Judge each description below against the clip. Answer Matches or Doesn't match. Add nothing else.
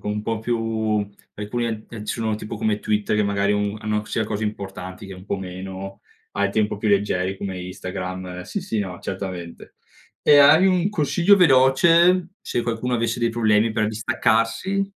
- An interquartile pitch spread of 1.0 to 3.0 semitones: Doesn't match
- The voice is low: Matches